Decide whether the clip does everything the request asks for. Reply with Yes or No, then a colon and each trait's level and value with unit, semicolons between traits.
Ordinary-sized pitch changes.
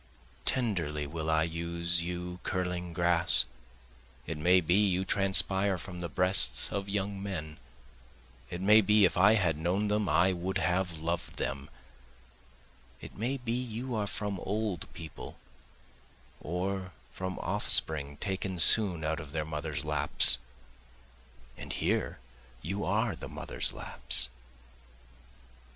Yes: average, 3.1 semitones